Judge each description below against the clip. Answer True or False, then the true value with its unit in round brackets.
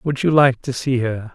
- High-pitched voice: False (130 Hz)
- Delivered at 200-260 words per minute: False (270 wpm)